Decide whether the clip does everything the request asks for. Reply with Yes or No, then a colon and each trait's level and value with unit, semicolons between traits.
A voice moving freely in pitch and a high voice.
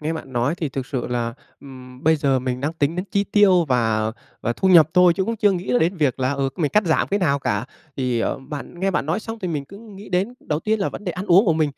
No: wide, 6.0 semitones; medium, 155 Hz